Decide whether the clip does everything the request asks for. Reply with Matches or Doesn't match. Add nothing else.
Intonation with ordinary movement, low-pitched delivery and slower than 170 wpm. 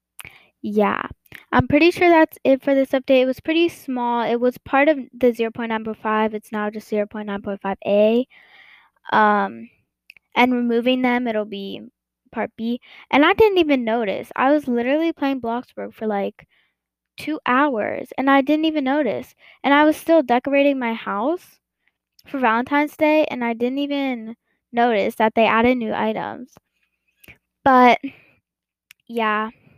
Doesn't match